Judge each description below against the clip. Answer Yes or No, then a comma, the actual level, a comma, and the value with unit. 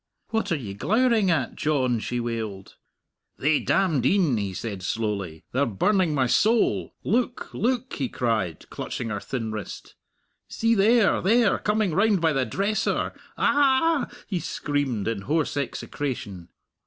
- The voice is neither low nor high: Yes, medium, 145 Hz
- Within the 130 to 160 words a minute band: Yes, average, 145 wpm